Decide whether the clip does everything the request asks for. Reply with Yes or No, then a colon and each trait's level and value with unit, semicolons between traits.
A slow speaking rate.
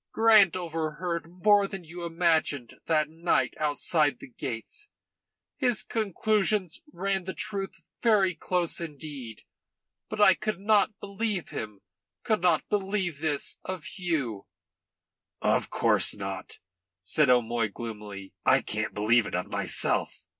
Yes: slow, 125 wpm